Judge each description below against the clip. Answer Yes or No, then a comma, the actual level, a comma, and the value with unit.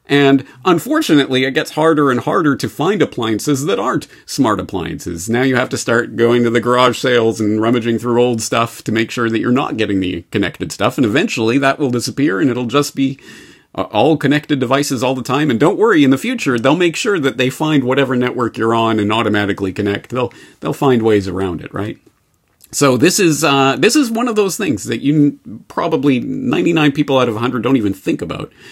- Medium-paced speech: No, fast, 215 wpm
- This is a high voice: No, low, 125 Hz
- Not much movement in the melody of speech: No, average, 4.1 semitones